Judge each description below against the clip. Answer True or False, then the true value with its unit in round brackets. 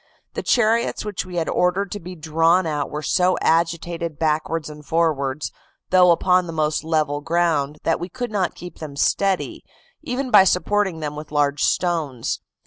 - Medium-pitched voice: True (165 Hz)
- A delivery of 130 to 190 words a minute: True (170 wpm)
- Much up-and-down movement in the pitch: False (3.3 semitones)